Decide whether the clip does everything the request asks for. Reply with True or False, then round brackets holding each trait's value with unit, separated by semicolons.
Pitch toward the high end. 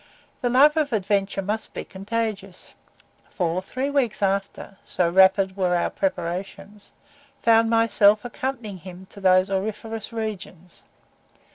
True (200 Hz)